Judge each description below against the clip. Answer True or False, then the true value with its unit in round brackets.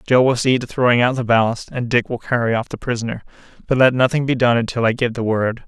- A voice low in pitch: True (120 Hz)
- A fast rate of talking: True (265 wpm)